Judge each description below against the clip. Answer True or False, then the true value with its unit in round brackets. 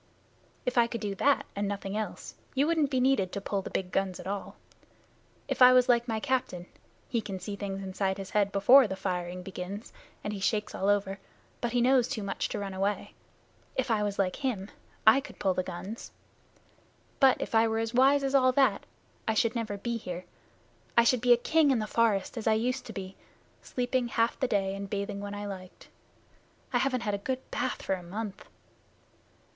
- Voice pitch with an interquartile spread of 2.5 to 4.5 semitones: True (4.1 semitones)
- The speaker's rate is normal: False (210 wpm)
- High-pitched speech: True (210 Hz)